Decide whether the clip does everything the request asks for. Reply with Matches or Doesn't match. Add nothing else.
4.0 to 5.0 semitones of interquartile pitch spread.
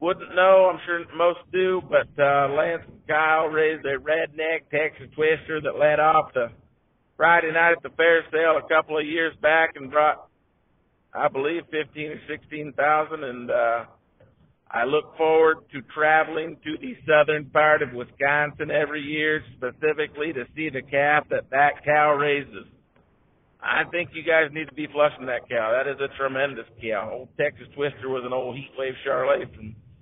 Doesn't match